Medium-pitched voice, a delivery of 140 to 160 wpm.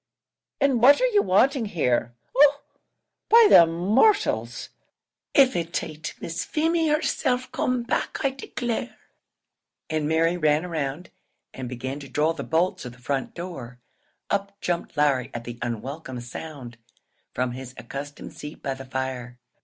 Yes: medium, 160 Hz; average, 150 wpm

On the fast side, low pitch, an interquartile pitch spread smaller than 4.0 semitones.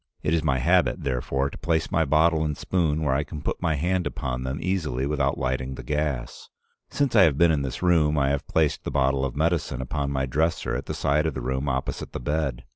Yes: fast, 235 wpm; very low, 70 Hz; average, 3.1 semitones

